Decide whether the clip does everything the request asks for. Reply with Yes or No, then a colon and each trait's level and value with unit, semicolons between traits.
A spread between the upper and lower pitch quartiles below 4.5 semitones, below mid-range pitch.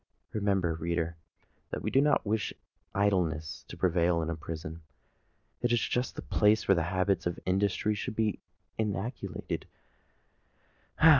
Yes: average, 4.1 semitones; very low, 95 Hz